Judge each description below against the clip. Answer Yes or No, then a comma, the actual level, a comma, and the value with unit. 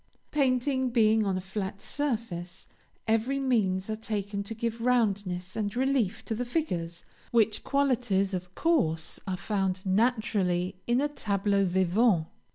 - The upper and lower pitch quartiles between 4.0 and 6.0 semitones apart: Yes, average, 4.4 semitones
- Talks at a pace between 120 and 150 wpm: Yes, average, 140 wpm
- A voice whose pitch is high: Yes, high, 215 Hz